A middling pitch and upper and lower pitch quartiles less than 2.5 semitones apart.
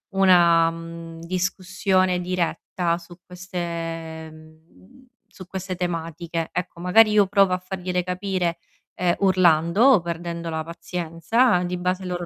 Yes: medium, 175 Hz; narrow, 1.8 semitones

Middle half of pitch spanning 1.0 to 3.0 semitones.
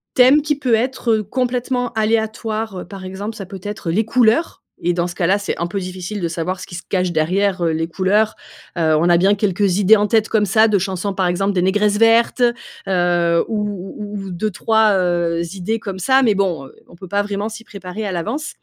No: average, 3.5 semitones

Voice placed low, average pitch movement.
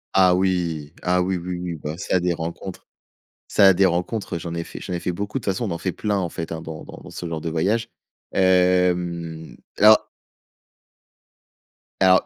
No: very low, 90 Hz; narrow, 2.0 semitones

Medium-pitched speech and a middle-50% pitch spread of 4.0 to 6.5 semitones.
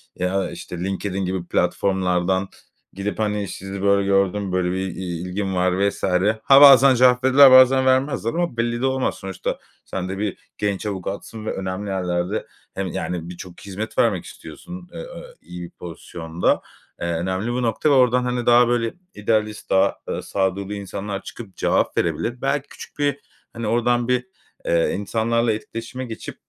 No: low, 100 Hz; average, 4.5 semitones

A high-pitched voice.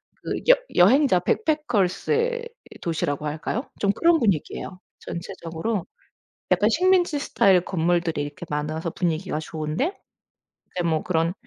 No: medium, 180 Hz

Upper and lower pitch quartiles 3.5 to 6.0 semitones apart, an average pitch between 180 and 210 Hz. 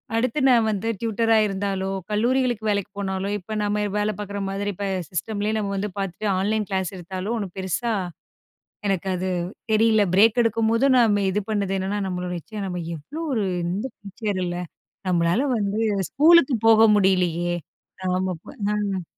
No: average, 2.8 semitones; high, 205 Hz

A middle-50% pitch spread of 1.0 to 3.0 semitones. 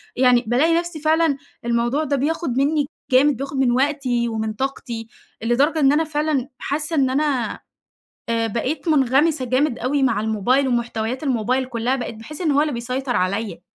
No: average, 3.7 semitones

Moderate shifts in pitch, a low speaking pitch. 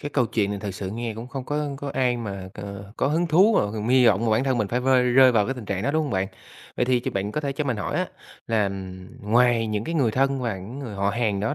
Yes: average, 4.4 semitones; low, 120 Hz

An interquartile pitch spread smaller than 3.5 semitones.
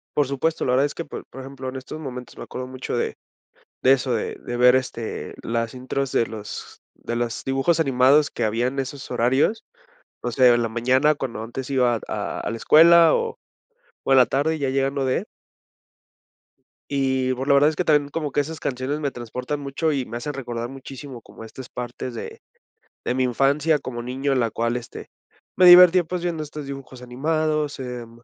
Yes: average, 2.9 semitones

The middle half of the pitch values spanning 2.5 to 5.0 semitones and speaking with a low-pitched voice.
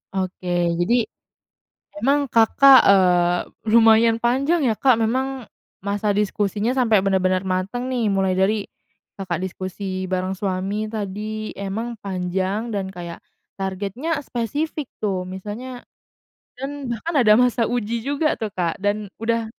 No: average, 4.1 semitones; high, 210 Hz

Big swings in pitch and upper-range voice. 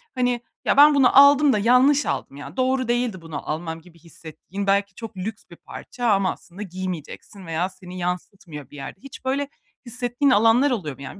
Yes: wide, 6.3 semitones; high, 200 Hz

